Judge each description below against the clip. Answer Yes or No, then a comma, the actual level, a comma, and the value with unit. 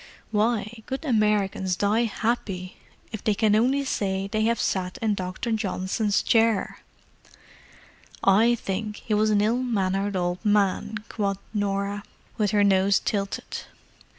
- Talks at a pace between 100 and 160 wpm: Yes, slow, 135 wpm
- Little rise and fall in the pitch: Yes, narrow, 2.3 semitones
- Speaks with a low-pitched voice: No, high, 210 Hz